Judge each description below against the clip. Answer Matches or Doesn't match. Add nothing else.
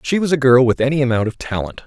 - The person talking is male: Matches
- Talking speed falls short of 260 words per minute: Doesn't match